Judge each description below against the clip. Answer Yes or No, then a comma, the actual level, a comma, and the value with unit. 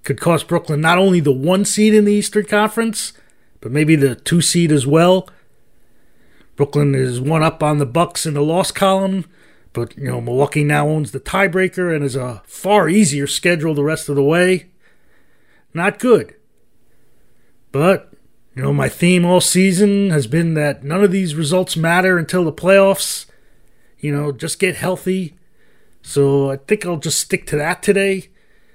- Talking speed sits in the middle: Yes, average, 175 wpm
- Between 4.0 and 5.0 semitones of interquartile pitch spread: Yes, average, 4.6 semitones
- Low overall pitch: No, medium, 170 Hz